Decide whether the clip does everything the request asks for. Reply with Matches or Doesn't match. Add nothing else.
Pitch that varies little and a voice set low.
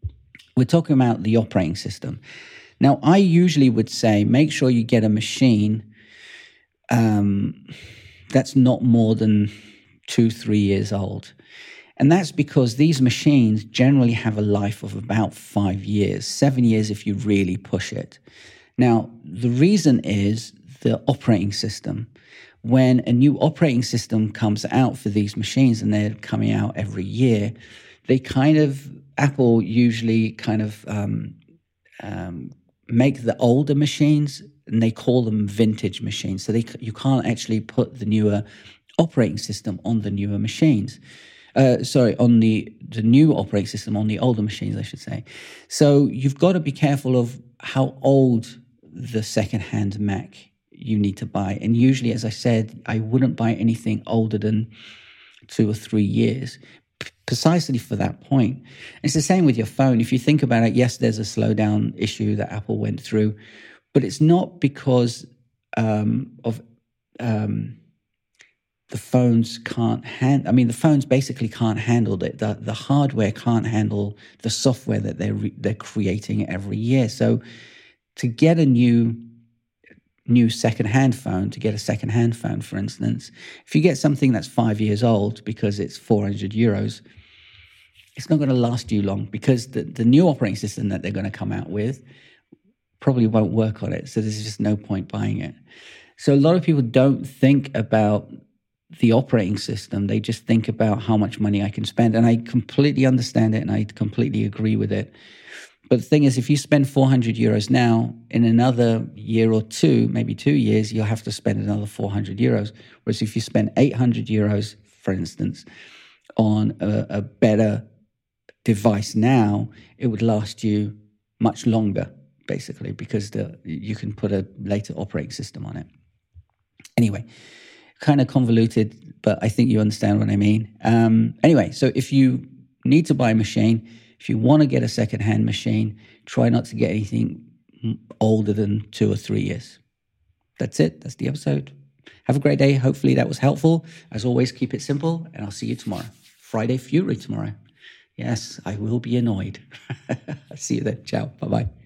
Doesn't match